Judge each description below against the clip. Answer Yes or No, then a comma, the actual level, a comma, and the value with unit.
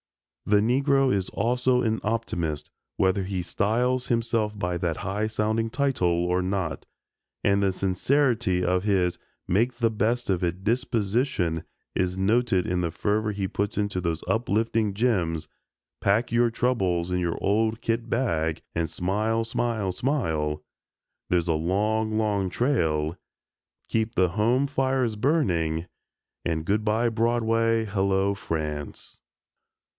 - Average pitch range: Yes, average, 4.3 semitones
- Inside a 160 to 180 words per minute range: No, slow, 135 wpm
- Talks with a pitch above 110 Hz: No, low, 105 Hz